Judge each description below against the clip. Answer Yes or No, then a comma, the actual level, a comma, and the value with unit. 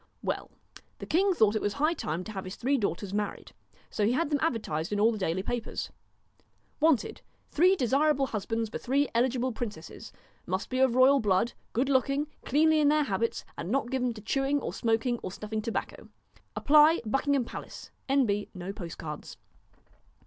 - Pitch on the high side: Yes, high, 240 Hz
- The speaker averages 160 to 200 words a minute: Yes, average, 180 wpm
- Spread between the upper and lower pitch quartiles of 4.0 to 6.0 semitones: Yes, average, 5.2 semitones